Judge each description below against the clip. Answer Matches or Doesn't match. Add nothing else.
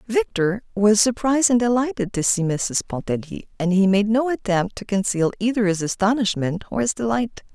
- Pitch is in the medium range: Doesn't match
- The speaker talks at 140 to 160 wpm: Doesn't match